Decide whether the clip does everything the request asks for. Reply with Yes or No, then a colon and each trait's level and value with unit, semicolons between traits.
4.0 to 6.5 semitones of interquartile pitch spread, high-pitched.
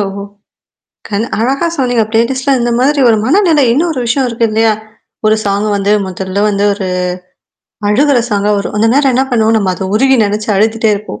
Yes: average, 4.4 semitones; high, 225 Hz